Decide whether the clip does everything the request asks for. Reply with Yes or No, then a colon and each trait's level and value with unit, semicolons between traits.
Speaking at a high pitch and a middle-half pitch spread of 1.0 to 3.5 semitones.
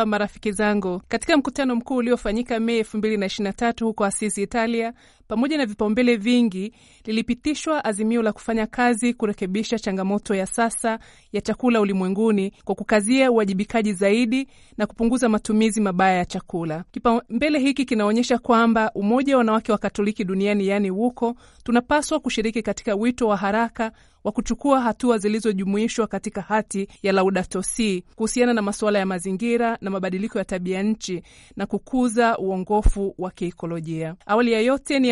Yes: high, 220 Hz; average, 2.9 semitones